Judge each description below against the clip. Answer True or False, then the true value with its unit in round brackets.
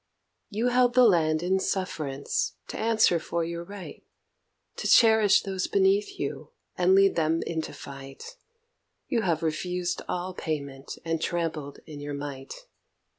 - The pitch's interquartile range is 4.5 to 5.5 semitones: True (4.9 semitones)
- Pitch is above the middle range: False (175 Hz)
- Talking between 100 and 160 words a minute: True (140 wpm)